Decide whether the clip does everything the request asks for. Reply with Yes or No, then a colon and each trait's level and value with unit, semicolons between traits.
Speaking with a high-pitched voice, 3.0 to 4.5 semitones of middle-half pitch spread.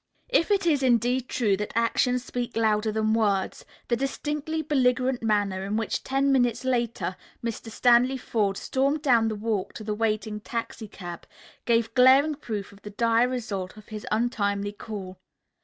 Yes: high, 230 Hz; average, 3.4 semitones